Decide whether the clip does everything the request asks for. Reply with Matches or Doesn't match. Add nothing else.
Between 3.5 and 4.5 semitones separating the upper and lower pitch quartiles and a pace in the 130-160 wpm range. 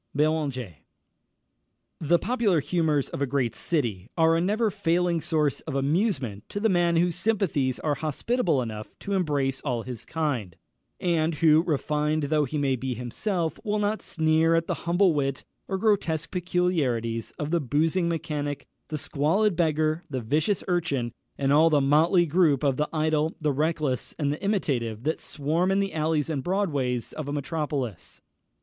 Doesn't match